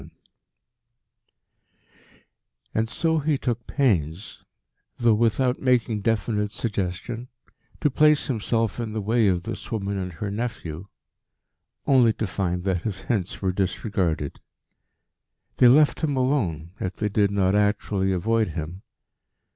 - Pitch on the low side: Yes, low, 105 Hz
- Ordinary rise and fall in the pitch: Yes, average, 4.2 semitones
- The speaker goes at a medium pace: No, slow, 130 wpm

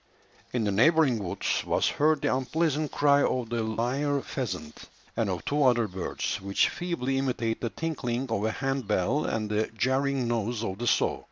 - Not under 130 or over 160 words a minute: No, average, 180 wpm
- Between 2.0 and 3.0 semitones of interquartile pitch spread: No, average, 4.1 semitones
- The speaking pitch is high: No, low, 120 Hz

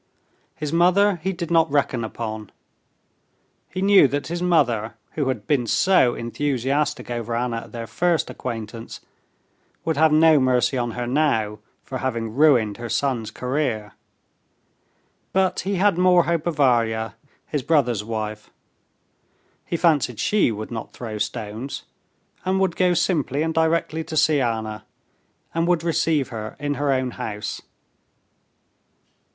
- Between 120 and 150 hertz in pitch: Yes, low, 135 Hz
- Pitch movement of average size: No, wide, 6.0 semitones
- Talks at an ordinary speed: Yes, average, 145 wpm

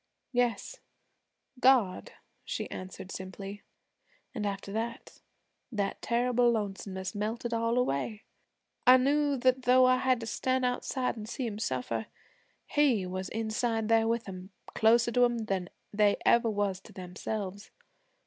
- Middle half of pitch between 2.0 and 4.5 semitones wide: Yes, average, 3.9 semitones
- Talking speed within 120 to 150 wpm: Yes, average, 140 wpm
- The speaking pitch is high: Yes, high, 225 Hz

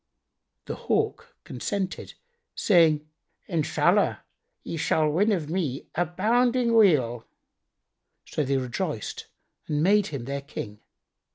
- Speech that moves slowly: Yes, slow, 105 wpm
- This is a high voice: No, medium, 160 Hz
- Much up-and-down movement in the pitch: Yes, wide, 5.9 semitones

